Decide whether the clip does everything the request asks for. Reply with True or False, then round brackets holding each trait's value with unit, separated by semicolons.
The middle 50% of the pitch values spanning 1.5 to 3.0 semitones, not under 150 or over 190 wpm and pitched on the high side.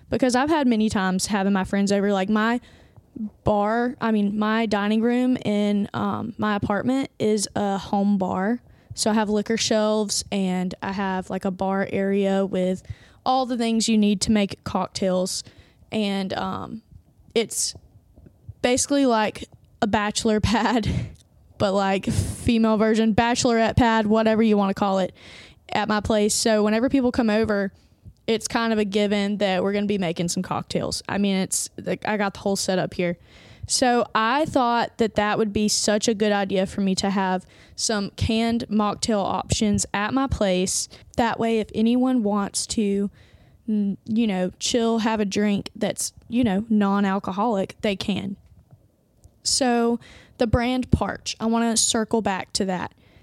True (2.4 semitones; 165 wpm; 210 Hz)